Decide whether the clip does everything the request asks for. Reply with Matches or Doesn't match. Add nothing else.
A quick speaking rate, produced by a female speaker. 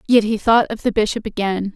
Matches